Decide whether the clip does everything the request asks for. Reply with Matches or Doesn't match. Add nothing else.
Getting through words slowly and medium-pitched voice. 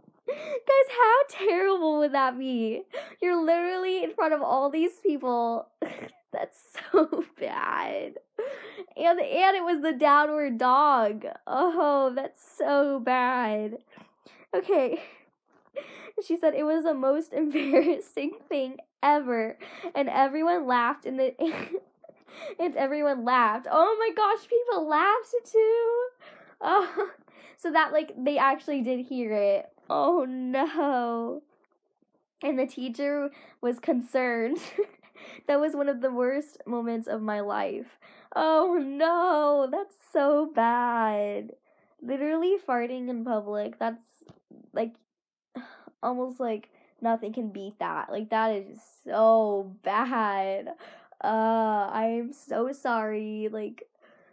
Doesn't match